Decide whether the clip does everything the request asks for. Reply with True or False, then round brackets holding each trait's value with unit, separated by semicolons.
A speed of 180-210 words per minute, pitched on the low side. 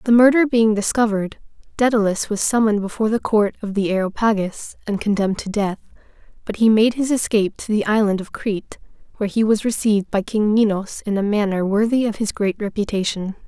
False (185 wpm; 210 Hz)